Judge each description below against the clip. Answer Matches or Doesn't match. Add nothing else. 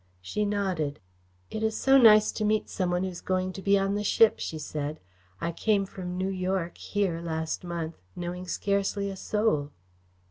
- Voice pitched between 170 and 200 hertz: Matches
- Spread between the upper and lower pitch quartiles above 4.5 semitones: Doesn't match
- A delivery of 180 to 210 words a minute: Matches